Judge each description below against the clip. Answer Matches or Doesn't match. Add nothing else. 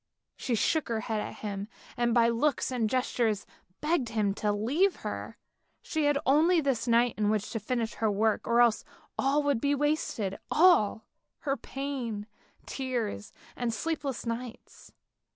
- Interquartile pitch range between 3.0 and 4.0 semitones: Doesn't match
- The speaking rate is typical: Matches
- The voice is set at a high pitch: Matches